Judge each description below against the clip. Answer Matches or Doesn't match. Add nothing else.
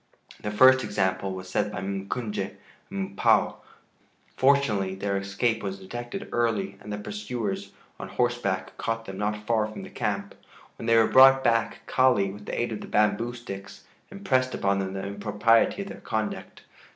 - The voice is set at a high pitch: Doesn't match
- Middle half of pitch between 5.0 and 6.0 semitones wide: Doesn't match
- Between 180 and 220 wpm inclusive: Doesn't match